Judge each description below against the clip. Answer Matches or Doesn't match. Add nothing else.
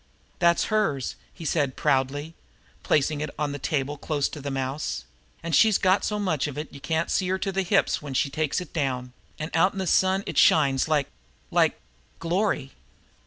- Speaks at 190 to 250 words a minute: Matches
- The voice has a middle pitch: Matches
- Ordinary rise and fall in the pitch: Matches